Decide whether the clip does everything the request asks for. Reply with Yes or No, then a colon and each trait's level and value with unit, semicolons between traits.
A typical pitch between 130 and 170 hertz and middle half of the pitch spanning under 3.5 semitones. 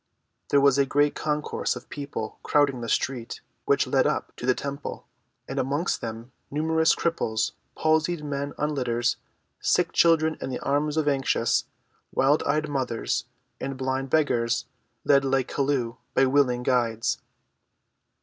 Yes: medium, 140 Hz; average, 2.9 semitones